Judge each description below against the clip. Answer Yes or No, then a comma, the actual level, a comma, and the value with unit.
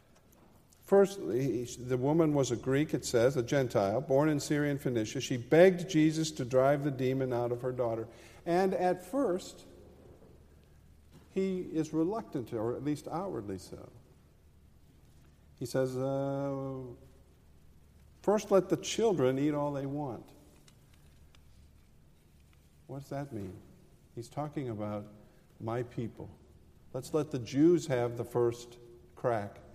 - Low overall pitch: Yes, low, 125 Hz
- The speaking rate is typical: No, slow, 130 wpm